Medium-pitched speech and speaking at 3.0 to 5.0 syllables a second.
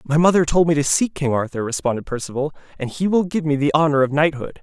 No: medium, 150 Hz; 6.4 syllables/s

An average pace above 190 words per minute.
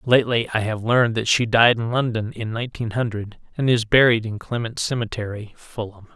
No: average, 185 wpm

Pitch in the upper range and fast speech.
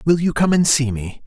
No: medium, 145 Hz; fast, 285 wpm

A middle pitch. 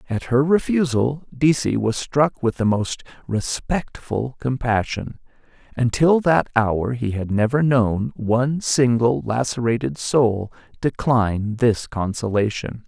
No: low, 120 Hz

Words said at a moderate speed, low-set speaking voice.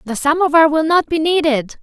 No: average, 195 wpm; very high, 305 Hz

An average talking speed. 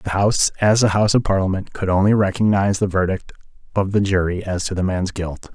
No: fast, 215 wpm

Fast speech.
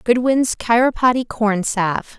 No: slow, 110 wpm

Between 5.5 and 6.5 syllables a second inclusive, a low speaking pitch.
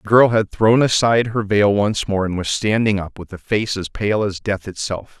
No: 4.9 syllables/s; low, 105 Hz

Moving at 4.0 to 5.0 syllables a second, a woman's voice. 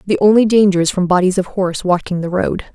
No: 6.1 syllables/s; female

